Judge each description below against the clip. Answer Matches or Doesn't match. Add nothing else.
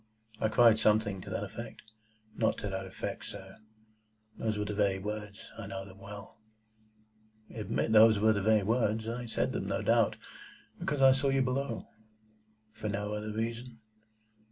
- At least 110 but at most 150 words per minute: Doesn't match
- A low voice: Matches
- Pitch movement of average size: Doesn't match